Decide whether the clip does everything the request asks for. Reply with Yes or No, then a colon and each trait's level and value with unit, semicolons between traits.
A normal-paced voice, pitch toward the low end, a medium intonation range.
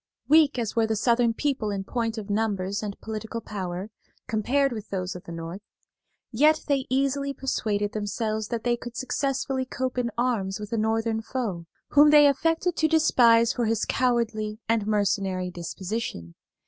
No: average, 165 wpm; high, 225 Hz; average, 4.0 semitones